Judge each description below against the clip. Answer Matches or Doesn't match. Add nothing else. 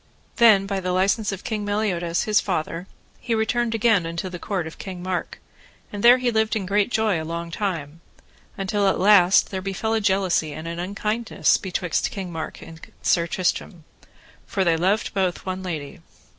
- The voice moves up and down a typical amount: Matches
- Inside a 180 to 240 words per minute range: Matches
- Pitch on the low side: Doesn't match